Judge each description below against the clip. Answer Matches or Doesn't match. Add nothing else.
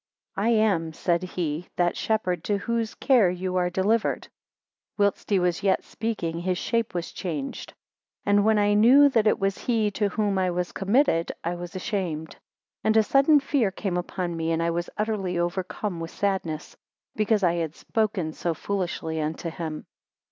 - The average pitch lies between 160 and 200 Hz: Matches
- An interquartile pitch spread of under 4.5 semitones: Matches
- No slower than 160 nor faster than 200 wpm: Matches